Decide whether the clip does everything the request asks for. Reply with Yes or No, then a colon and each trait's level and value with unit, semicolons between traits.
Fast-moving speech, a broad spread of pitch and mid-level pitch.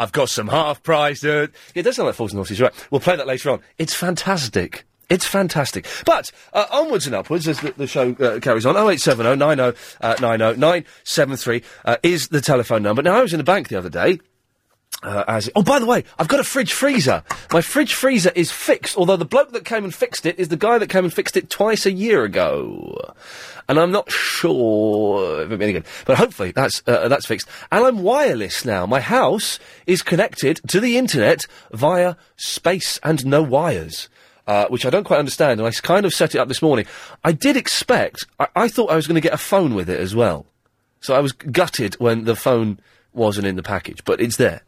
Yes: fast, 230 wpm; wide, 8.2 semitones; medium, 160 Hz